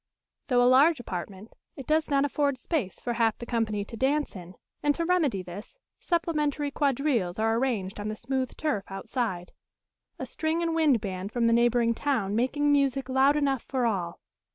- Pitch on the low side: No, very high, 250 Hz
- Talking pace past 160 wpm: Yes, average, 180 wpm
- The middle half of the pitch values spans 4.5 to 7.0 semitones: Yes, average, 5.2 semitones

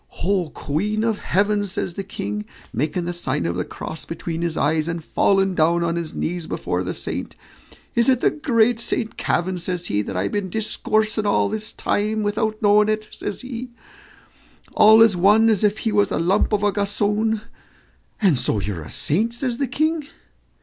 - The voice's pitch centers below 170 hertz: No, high, 205 Hz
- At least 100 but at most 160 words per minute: No, average, 190 wpm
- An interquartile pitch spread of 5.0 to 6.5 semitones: No, average, 4.3 semitones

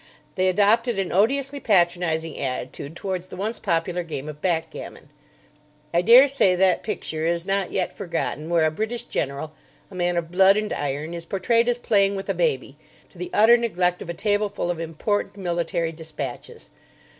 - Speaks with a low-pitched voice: No, medium, 180 Hz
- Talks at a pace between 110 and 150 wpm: No, average, 175 wpm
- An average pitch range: Yes, average, 4.1 semitones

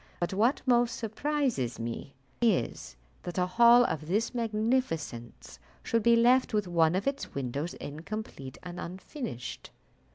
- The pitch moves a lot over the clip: Yes, wide, 7.2 semitones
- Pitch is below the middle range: No, high, 200 Hz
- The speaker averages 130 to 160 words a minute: Yes, slow, 135 wpm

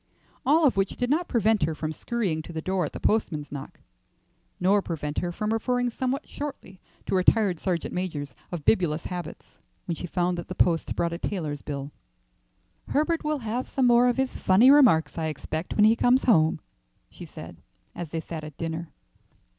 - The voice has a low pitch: No, medium, 185 Hz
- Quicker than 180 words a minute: Yes, average, 190 wpm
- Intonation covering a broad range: Yes, wide, 6.9 semitones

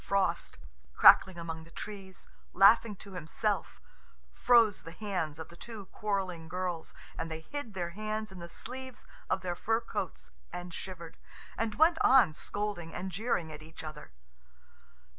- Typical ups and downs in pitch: Yes, average, 4.2 semitones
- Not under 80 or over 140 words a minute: No, average, 160 wpm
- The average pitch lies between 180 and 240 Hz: Yes, high, 190 Hz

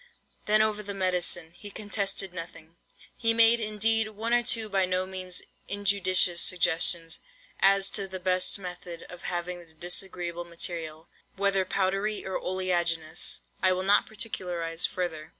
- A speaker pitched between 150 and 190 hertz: Yes, medium, 185 Hz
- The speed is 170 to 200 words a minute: No, average, 145 wpm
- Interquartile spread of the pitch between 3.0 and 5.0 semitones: No, narrow, 2.6 semitones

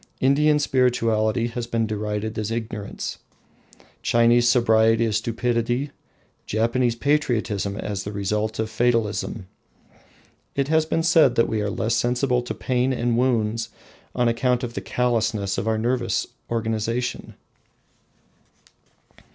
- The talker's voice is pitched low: Yes, low, 115 Hz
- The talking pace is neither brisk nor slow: No, slow, 125 wpm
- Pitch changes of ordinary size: No, narrow, 2.2 semitones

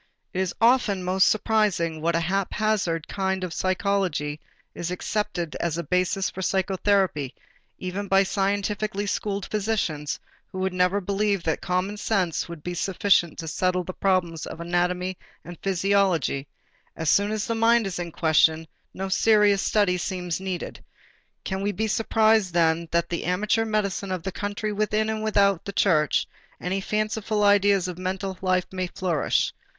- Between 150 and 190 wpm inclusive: Yes, average, 160 wpm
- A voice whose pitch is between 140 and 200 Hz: Yes, high, 190 Hz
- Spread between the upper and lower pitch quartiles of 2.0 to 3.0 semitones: Yes, narrow, 2.6 semitones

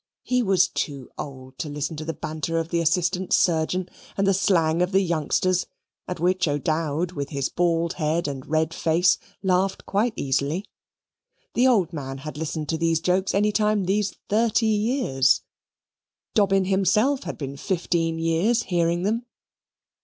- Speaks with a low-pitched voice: No, medium, 170 Hz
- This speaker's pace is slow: No, average, 160 wpm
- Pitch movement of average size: Yes, average, 3.7 semitones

